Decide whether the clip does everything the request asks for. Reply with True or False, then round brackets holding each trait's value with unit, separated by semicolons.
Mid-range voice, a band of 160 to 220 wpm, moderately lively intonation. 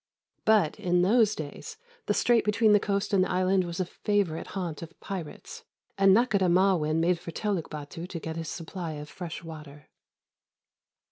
True (180 Hz; 175 wpm; 3.4 semitones)